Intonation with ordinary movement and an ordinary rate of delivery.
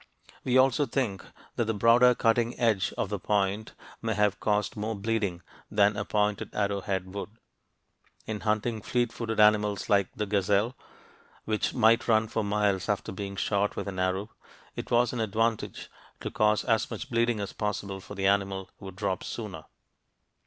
No: narrow, 2.2 semitones; average, 165 wpm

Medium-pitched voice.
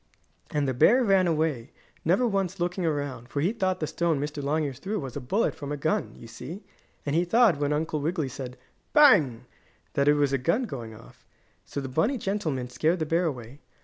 Yes: medium, 155 Hz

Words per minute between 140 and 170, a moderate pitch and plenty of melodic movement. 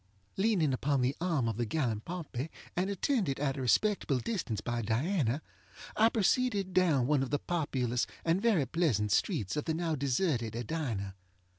Yes: average, 165 wpm; medium, 145 Hz; wide, 6.7 semitones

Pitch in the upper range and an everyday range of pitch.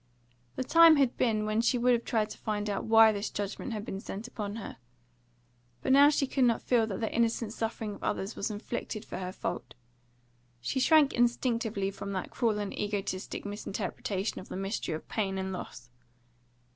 Yes: high, 215 Hz; average, 3.1 semitones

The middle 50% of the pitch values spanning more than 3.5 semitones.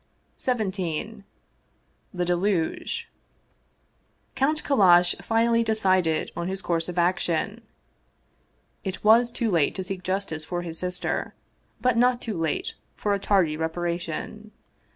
Yes: average, 4.1 semitones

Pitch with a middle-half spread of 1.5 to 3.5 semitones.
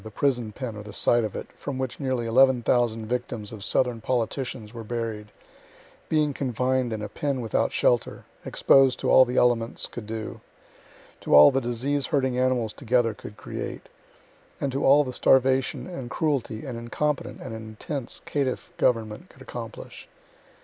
Yes: average, 2.8 semitones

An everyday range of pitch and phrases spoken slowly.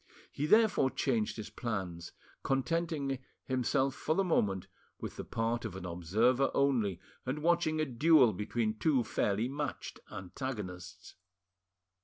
No: wide, 5.8 semitones; slow, 130 wpm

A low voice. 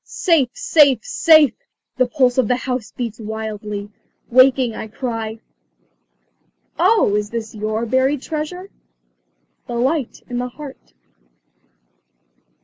No: very high, 250 Hz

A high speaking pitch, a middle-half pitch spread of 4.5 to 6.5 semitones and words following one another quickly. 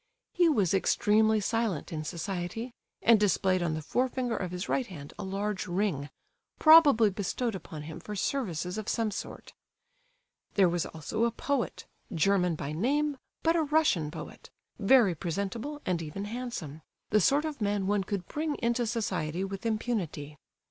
No: high, 205 Hz; average, 5.2 semitones; average, 155 wpm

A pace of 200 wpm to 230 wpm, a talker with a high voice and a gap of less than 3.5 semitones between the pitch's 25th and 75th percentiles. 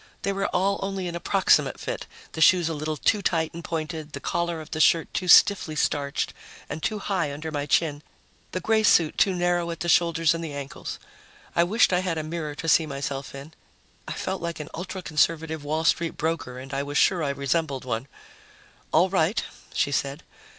No: fast, 205 wpm; medium, 160 Hz; average, 3.1 semitones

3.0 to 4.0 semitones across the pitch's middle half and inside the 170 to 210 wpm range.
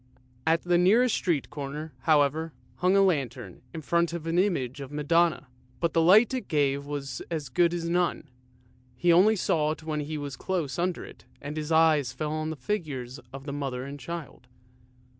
Yes: average, 3.4 semitones; average, 195 wpm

